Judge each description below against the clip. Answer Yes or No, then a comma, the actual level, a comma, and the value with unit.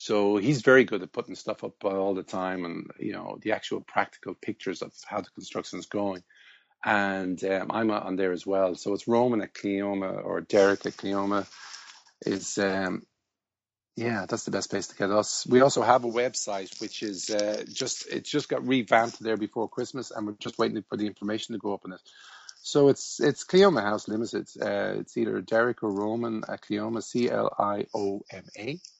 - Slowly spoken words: No, average, 195 wpm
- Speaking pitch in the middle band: No, low, 105 Hz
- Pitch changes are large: No, average, 3.1 semitones